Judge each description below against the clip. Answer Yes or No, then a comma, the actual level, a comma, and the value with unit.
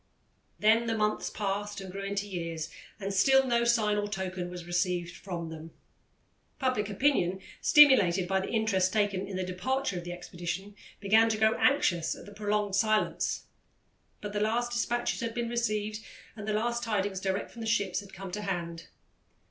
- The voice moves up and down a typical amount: Yes, average, 3.1 semitones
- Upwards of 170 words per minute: Yes, average, 180 wpm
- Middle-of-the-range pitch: No, high, 205 Hz